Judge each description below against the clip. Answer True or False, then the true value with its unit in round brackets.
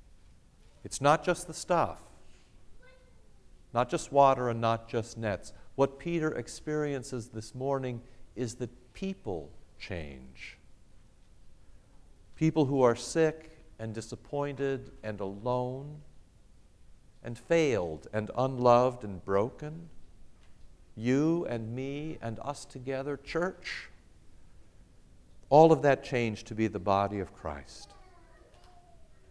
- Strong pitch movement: True (5.8 semitones)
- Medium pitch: False (120 Hz)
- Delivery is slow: True (105 wpm)